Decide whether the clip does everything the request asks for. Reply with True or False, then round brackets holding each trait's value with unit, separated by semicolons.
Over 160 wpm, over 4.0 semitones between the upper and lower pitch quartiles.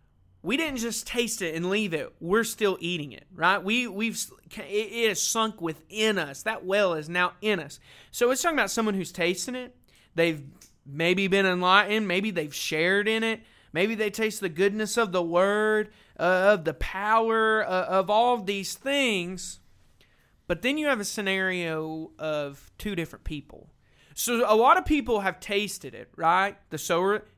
True (180 wpm; 4.7 semitones)